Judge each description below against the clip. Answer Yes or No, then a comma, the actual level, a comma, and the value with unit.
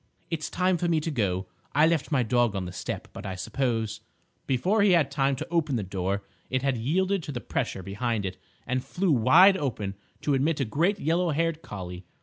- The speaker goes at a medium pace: No, fast, 210 wpm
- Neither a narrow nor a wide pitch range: No, wide, 7.6 semitones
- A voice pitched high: No, low, 135 Hz